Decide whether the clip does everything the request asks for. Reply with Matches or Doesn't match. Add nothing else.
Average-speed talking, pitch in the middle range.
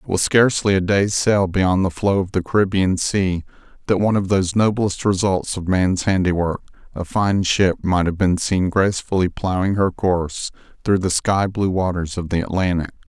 Doesn't match